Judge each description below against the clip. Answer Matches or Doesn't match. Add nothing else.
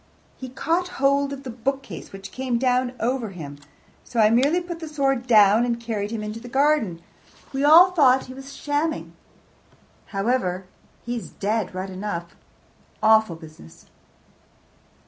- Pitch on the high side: Matches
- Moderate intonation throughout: Matches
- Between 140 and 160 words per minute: Matches